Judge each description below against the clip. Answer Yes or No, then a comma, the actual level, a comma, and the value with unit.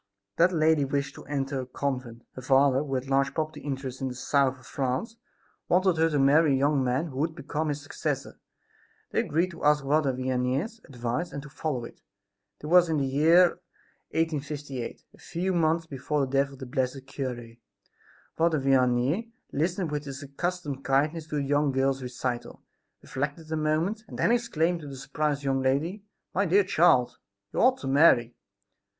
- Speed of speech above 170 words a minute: Yes, average, 180 wpm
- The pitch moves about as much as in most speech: Yes, average, 3.3 semitones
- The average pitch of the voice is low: No, medium, 145 Hz